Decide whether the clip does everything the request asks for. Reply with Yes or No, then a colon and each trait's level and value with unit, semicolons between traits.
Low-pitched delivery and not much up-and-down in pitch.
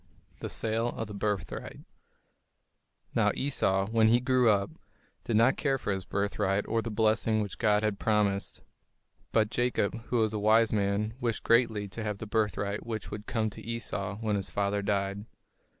Yes: low, 110 Hz; narrow, 2.0 semitones